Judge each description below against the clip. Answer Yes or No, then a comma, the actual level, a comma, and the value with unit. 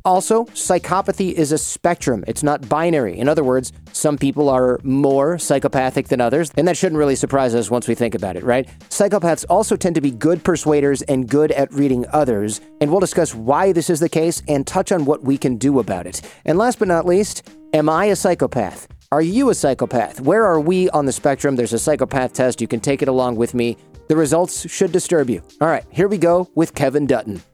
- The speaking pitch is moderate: Yes, medium, 150 Hz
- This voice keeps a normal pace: No, fast, 220 wpm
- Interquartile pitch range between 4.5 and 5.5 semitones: Yes, average, 5.0 semitones